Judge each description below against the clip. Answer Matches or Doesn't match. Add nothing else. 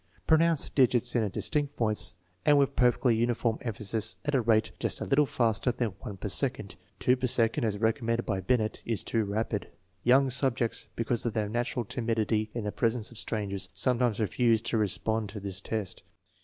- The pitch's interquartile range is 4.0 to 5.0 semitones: Doesn't match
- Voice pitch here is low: Matches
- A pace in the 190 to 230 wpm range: Matches